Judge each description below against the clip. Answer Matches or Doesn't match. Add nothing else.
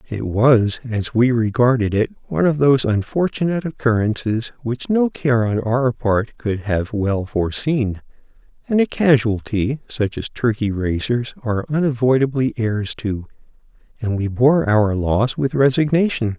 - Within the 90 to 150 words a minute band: Matches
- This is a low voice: Matches